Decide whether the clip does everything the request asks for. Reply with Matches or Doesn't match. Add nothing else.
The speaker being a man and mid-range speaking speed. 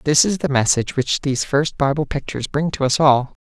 Doesn't match